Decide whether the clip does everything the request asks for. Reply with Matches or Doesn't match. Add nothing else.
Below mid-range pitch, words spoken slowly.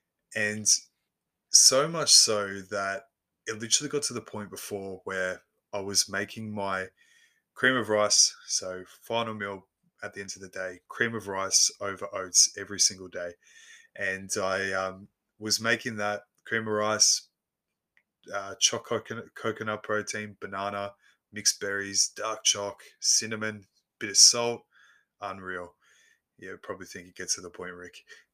Doesn't match